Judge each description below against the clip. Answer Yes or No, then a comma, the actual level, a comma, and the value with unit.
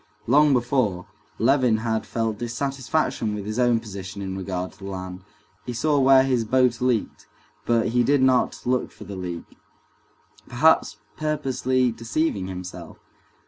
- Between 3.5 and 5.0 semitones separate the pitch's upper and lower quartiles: Yes, average, 4.5 semitones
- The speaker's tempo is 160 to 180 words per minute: No, average, 145 wpm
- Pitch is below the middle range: Yes, low, 120 Hz